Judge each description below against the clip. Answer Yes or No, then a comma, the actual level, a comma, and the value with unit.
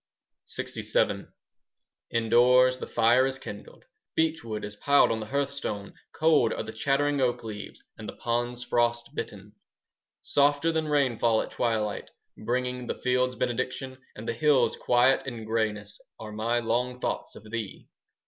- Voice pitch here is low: Yes, low, 120 Hz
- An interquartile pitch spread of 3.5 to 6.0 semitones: No, average, 2.9 semitones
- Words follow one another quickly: No, average, 150 wpm